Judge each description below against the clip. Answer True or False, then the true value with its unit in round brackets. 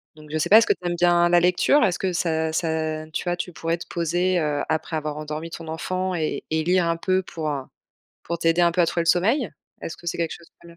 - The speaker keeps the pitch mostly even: True (1.9 semitones)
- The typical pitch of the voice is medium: True (170 Hz)